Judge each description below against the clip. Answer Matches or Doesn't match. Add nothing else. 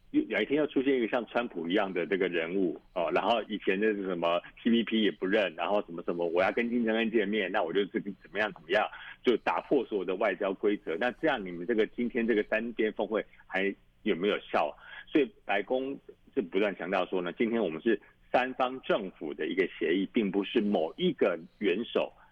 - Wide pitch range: Doesn't match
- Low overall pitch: Matches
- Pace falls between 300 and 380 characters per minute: Matches